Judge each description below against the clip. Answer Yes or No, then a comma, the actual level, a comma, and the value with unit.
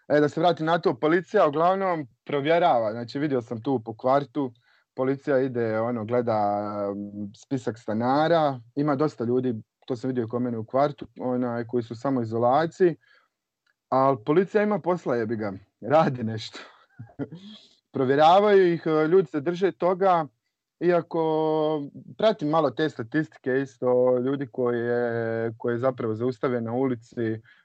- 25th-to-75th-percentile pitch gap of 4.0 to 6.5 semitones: Yes, average, 4.6 semitones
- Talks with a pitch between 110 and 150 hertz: Yes, low, 135 Hz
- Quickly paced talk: No, average, 135 wpm